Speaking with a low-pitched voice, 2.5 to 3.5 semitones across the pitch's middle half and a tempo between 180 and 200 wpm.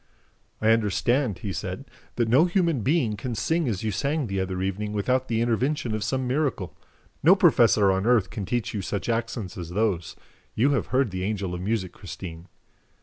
No: low, 110 Hz; average, 4.8 semitones; average, 190 wpm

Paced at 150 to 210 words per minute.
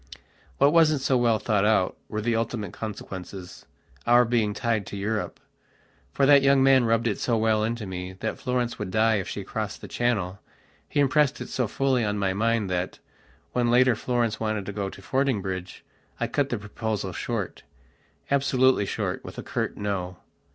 Yes: average, 170 wpm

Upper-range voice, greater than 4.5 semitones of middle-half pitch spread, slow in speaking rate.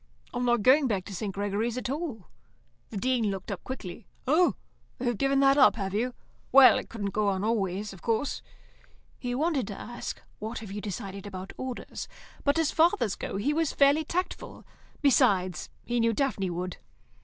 No: high, 230 Hz; wide, 5.4 semitones; average, 180 wpm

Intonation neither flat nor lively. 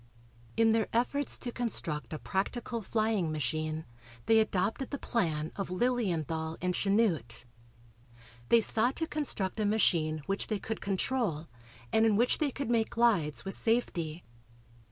No: wide, 6.3 semitones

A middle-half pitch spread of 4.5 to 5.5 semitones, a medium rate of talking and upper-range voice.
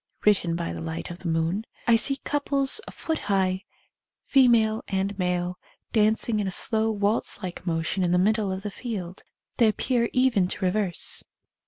No: average, 3.7 semitones; average, 185 wpm; high, 200 Hz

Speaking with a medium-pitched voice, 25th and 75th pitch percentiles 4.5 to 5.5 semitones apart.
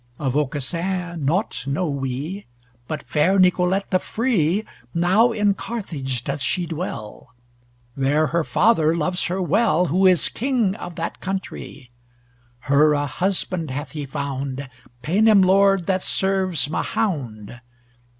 Yes: medium, 170 Hz; average, 5.2 semitones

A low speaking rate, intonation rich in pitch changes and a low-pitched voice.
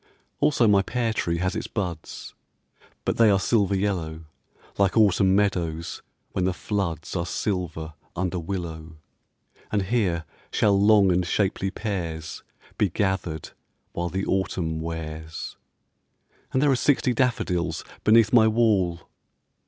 No: slow, 130 wpm; average, 3.7 semitones; very low, 95 Hz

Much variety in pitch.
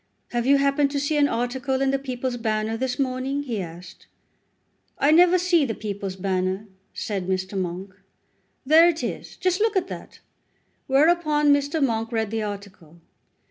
Yes: wide, 6.0 semitones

